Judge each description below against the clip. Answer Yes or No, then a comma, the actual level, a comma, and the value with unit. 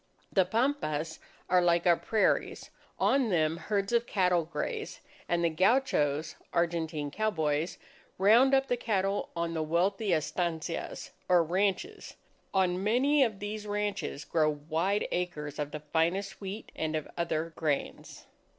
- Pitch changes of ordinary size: Yes, average, 4.5 semitones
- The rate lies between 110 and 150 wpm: Yes, average, 140 wpm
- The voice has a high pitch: No, medium, 180 Hz